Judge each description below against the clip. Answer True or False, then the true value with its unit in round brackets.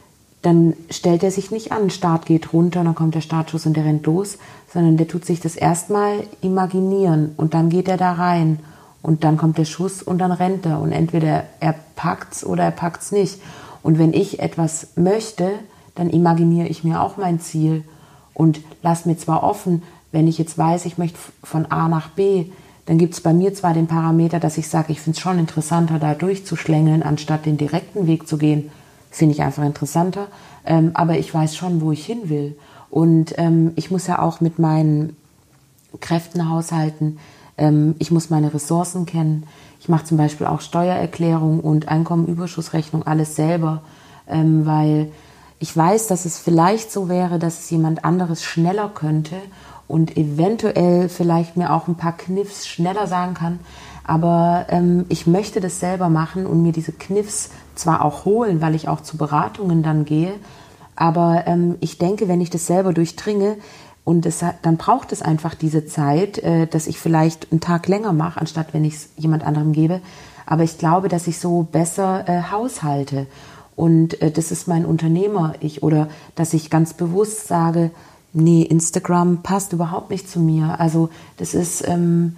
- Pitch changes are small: True (2.0 semitones)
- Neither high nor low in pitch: True (165 Hz)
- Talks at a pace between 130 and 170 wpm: False (180 wpm)